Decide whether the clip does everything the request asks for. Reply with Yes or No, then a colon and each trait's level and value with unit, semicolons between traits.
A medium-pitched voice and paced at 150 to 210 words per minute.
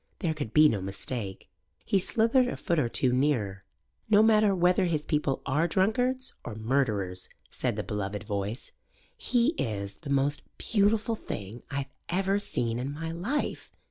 Yes: medium, 145 Hz; average, 160 wpm